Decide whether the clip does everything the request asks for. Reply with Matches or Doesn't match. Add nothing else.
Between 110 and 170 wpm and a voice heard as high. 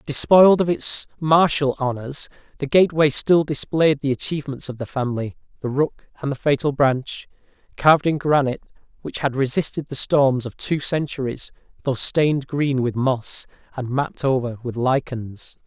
Doesn't match